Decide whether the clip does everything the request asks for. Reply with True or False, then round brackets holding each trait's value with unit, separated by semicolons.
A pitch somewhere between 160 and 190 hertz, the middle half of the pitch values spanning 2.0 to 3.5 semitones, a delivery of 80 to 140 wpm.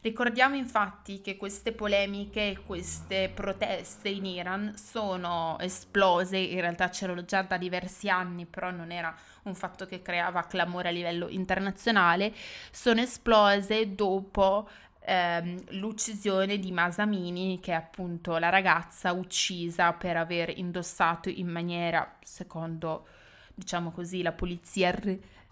True (185 Hz; 2.5 semitones; 130 wpm)